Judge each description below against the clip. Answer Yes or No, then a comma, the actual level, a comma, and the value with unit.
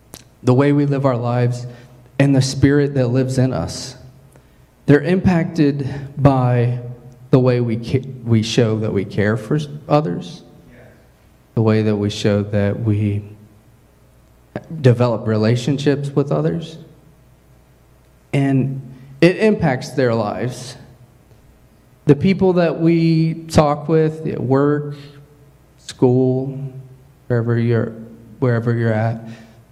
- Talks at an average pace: No, slow, 115 wpm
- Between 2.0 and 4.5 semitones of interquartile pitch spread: Yes, average, 3.8 semitones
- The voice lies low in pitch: Yes, low, 130 Hz